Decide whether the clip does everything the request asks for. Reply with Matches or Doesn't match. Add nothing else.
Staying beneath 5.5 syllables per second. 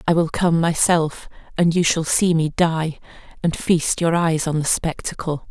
Matches